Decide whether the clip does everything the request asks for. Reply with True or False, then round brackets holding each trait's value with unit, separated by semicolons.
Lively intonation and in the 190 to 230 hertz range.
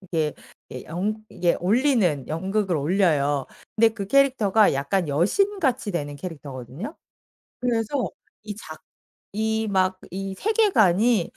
True (5.8 semitones; 195 Hz)